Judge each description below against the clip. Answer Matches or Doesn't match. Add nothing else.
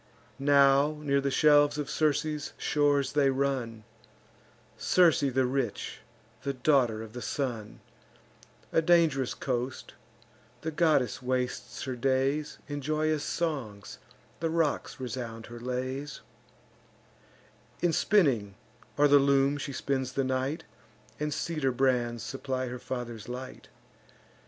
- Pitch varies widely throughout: Doesn't match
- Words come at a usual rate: Doesn't match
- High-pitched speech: Doesn't match